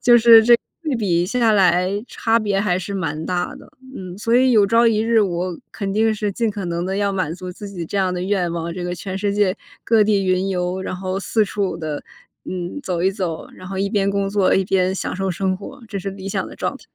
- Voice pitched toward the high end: Yes, high, 195 Hz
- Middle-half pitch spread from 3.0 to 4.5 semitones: No, narrow, 2.4 semitones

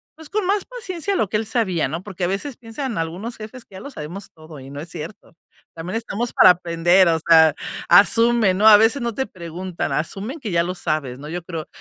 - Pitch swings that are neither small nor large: No, wide, 5.7 semitones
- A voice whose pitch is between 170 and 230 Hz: Yes, high, 190 Hz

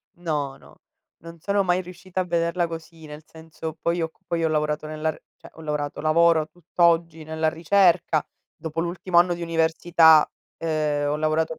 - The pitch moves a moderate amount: No, narrow, 1.6 semitones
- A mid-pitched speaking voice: Yes, medium, 165 Hz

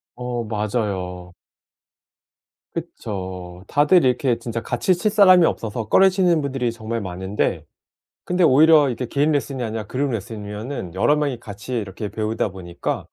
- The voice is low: Yes, low, 115 Hz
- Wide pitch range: Yes, wide, 5.7 semitones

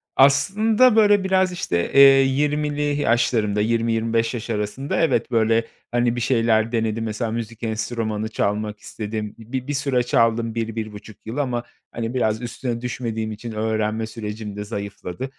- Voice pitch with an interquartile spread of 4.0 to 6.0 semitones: No, average, 2.7 semitones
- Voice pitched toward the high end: No, low, 115 Hz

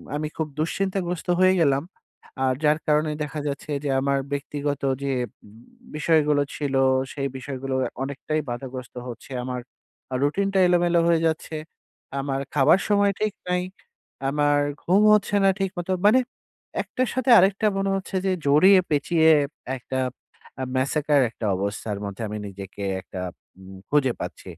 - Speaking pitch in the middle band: Yes, medium, 150 Hz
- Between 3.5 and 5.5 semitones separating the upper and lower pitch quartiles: Yes, average, 4.9 semitones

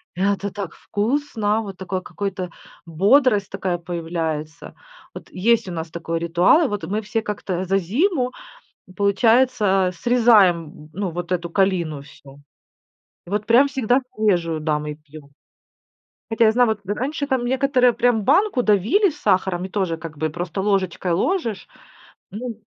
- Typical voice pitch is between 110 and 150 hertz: No, high, 200 Hz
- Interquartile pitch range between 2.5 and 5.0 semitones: No, wide, 5.4 semitones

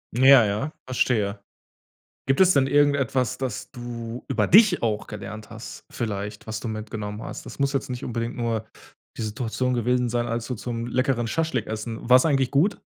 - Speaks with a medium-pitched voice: No, low, 120 Hz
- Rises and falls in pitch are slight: No, average, 3.2 semitones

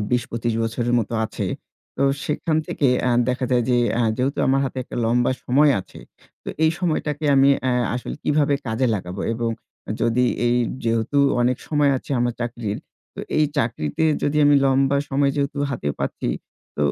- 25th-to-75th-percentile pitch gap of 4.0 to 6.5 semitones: No, average, 3.2 semitones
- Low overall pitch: Yes, low, 125 Hz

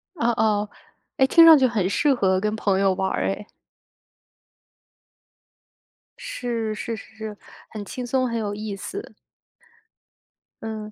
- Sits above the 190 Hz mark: Yes, high, 220 Hz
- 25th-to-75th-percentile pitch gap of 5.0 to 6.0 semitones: No, average, 3.1 semitones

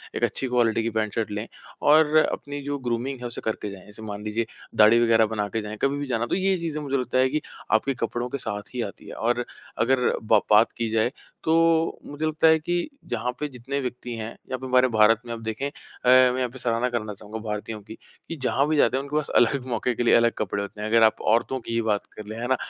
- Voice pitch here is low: Yes, low, 120 Hz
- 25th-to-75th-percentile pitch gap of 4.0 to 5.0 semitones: No, average, 3.6 semitones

